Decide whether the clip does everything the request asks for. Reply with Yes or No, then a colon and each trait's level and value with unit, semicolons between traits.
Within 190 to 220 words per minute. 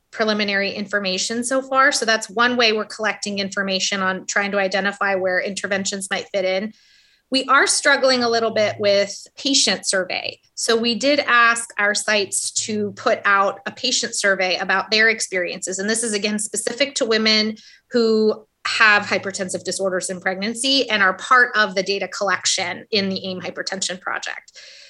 No: average, 165 wpm